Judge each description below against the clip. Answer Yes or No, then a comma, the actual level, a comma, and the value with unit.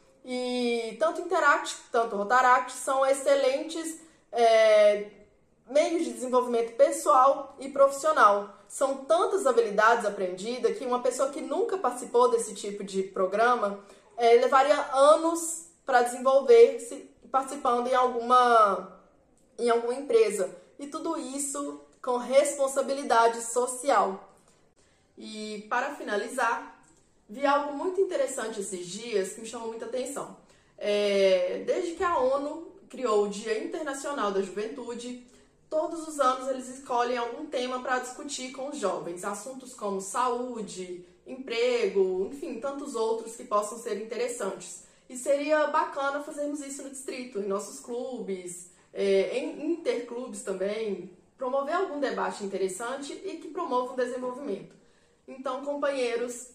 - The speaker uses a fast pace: No, average, 125 wpm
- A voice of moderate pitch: No, very high, 255 Hz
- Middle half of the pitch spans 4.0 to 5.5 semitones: Yes, average, 4.4 semitones